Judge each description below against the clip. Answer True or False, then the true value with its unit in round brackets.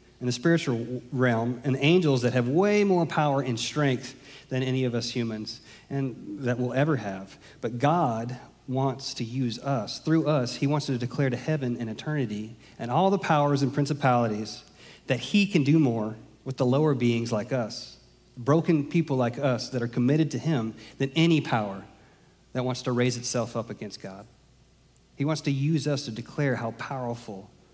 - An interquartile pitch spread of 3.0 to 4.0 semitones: True (3.4 semitones)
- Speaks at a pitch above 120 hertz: True (130 Hz)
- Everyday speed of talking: True (185 wpm)